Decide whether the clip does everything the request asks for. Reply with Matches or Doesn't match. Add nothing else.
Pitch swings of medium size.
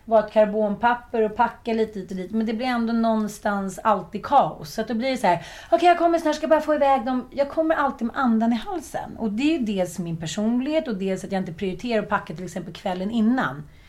Matches